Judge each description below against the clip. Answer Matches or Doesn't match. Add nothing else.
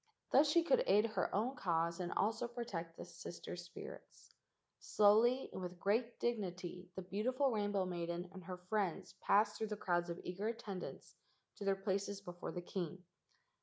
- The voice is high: Matches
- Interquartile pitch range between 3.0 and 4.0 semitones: Matches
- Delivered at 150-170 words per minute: Matches